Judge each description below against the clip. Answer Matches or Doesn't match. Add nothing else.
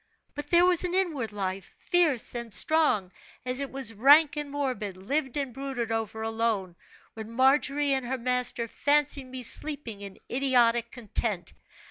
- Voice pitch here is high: Matches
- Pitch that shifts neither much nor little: Matches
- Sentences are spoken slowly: Doesn't match